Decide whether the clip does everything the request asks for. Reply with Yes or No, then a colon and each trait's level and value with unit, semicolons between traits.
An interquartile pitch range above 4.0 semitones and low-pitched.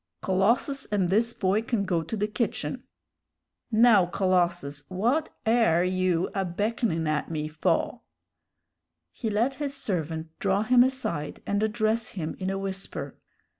No: average, 4.6 semitones; high, 195 Hz